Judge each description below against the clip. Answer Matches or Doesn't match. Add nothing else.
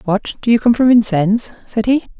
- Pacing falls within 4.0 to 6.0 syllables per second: Matches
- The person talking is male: Doesn't match